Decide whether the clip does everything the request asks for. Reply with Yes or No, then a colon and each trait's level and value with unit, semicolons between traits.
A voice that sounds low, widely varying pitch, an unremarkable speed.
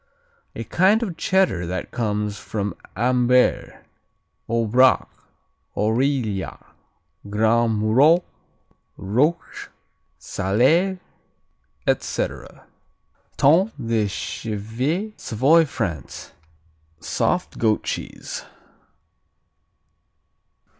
No: low, 120 Hz; wide, 6.7 semitones; slow, 65 wpm